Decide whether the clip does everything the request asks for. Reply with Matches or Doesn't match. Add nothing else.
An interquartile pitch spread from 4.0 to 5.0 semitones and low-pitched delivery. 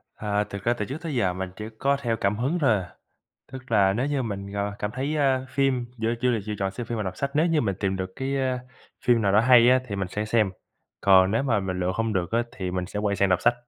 Matches